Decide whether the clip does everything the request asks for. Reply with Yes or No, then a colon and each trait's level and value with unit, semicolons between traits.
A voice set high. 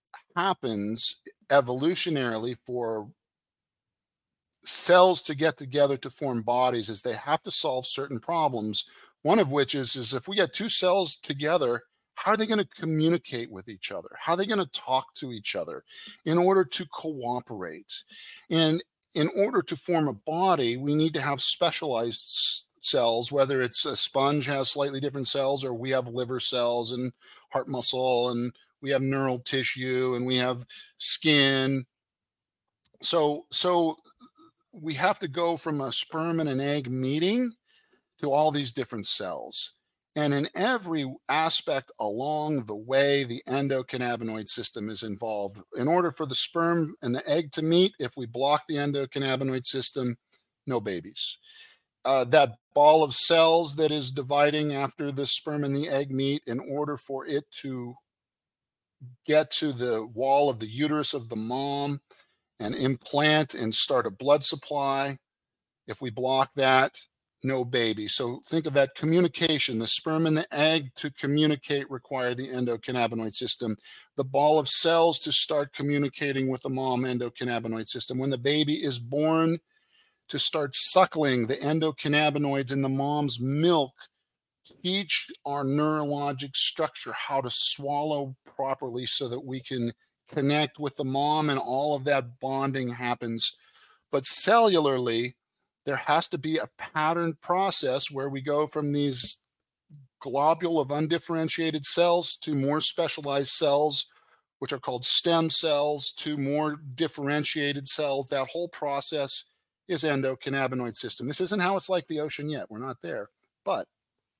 No: medium, 140 Hz